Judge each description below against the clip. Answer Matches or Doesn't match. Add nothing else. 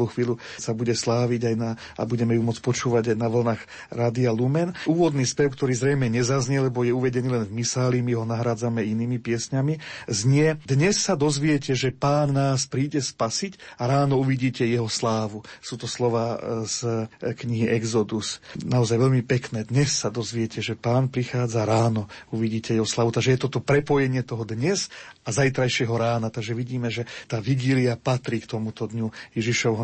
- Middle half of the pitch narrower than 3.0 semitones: Matches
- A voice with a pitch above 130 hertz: Doesn't match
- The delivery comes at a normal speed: Doesn't match